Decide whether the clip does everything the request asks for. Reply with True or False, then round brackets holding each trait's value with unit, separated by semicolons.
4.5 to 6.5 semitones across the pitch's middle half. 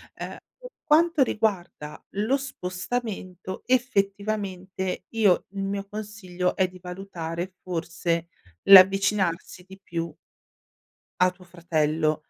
False (2.8 semitones)